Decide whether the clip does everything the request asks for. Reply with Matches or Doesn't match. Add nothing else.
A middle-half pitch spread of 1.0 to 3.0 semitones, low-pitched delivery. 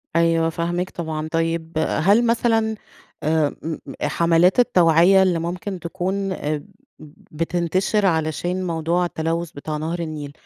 Doesn't match